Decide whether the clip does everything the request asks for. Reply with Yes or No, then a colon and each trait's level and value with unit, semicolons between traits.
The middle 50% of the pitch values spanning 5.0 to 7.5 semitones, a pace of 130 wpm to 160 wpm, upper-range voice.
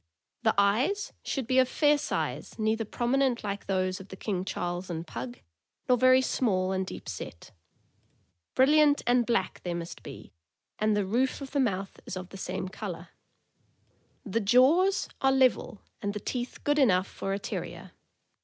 No: wide, 5.5 semitones; average, 170 wpm; high, 215 Hz